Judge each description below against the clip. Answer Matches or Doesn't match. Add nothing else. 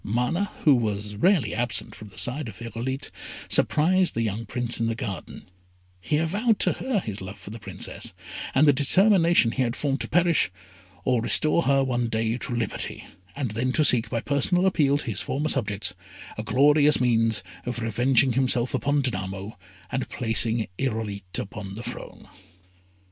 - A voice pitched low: Matches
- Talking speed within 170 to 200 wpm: Matches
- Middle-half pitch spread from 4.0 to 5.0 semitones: Matches